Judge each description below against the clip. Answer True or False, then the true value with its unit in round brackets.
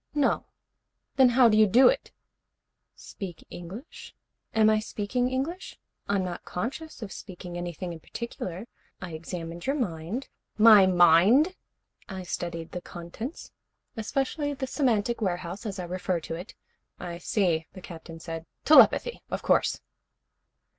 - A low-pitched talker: False (195 Hz)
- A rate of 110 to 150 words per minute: True (145 wpm)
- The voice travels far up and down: True (5.9 semitones)